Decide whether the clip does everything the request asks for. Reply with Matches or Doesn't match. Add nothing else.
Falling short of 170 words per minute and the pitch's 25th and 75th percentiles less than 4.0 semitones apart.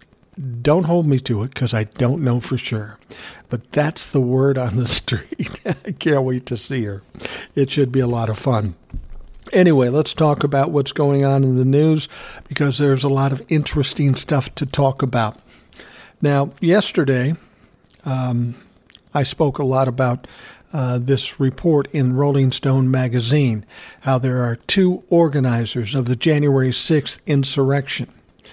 Matches